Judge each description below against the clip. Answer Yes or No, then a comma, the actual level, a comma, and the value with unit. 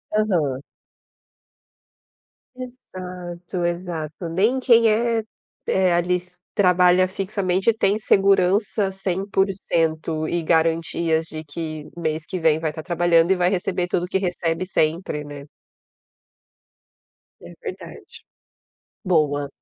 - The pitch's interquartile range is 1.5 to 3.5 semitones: Yes, average, 2.9 semitones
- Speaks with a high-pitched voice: No, medium, 180 Hz